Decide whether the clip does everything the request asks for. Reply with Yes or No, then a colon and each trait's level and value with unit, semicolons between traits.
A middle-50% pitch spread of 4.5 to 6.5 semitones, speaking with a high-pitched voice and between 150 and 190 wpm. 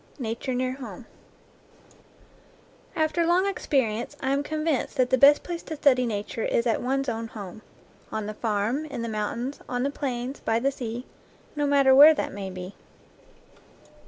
No: average, 4.1 semitones; very high, 255 Hz; average, 165 wpm